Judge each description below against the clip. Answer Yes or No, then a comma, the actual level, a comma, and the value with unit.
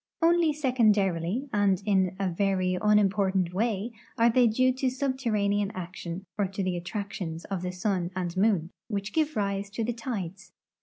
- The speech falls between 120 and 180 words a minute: Yes, average, 170 wpm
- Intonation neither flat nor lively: Yes, average, 3.8 semitones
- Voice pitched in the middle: No, high, 200 Hz